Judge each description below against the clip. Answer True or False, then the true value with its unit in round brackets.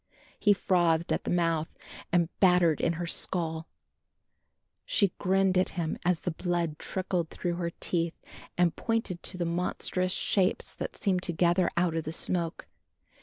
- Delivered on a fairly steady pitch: True (1.6 semitones)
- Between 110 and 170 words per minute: True (160 wpm)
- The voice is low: False (175 Hz)